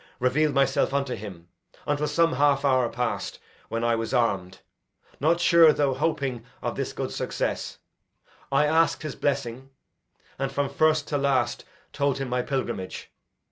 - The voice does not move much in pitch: No, average, 3.3 semitones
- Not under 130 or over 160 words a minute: Yes, average, 150 wpm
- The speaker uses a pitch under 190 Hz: Yes, low, 135 Hz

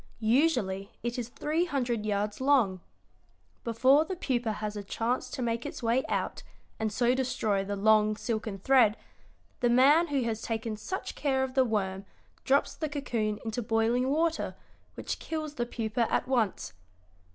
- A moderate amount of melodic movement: Yes, average, 3.6 semitones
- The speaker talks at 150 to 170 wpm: Yes, average, 165 wpm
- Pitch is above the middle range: Yes, high, 235 Hz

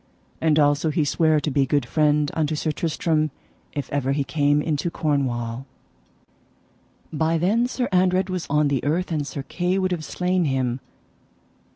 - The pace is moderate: Yes, average, 165 wpm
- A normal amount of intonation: Yes, average, 3.0 semitones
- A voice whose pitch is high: No, medium, 150 Hz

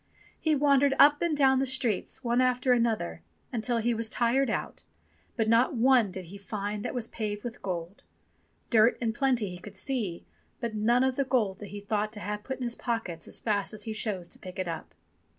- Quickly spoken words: Yes, fast, 215 wpm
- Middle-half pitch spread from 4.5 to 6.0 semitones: No, average, 3.8 semitones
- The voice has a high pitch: Yes, high, 225 Hz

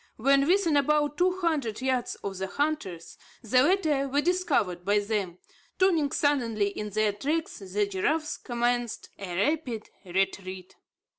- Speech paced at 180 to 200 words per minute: No, average, 140 wpm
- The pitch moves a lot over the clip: Yes, wide, 6.9 semitones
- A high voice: Yes, high, 245 Hz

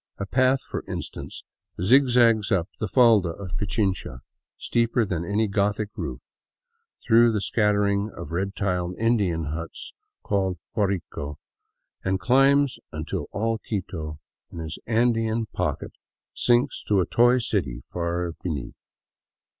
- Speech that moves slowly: Yes, slow, 125 wpm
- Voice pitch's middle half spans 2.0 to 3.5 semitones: No, average, 4.6 semitones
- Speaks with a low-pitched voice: Yes, low, 100 Hz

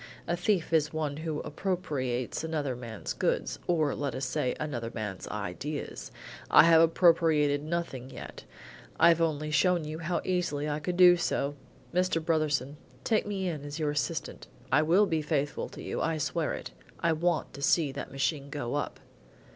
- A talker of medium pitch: Yes, medium, 155 Hz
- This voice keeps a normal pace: Yes, average, 170 wpm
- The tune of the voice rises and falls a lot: No, average, 3.0 semitones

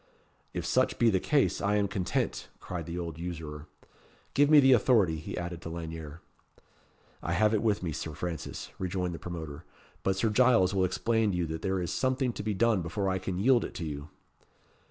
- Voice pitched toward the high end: No, very low, 90 Hz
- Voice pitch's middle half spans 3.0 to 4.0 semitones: No, average, 4.5 semitones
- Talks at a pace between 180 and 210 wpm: Yes, fast, 205 wpm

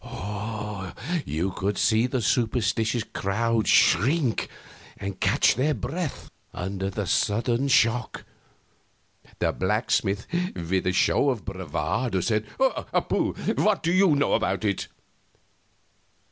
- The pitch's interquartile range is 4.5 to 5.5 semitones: Yes, average, 4.9 semitones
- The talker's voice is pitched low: Yes, low, 110 Hz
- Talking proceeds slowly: Yes, slow, 110 wpm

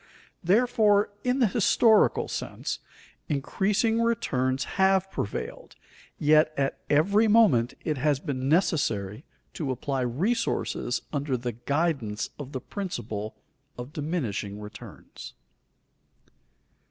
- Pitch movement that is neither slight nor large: No, wide, 7.8 semitones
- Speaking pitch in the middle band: Yes, medium, 150 Hz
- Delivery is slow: Yes, slow, 105 wpm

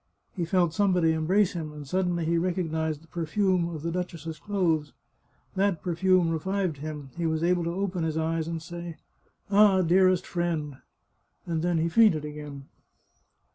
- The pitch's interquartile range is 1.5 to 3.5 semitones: Yes, narrow, 2.5 semitones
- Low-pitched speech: No, medium, 170 Hz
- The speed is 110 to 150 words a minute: No, average, 175 wpm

